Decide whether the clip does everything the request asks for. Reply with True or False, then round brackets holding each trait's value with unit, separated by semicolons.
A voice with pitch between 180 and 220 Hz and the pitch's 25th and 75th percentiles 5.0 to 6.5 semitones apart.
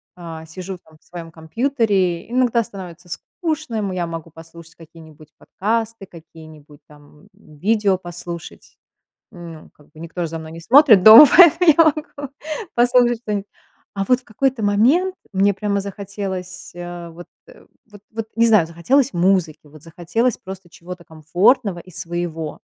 True (185 Hz; 5.3 semitones)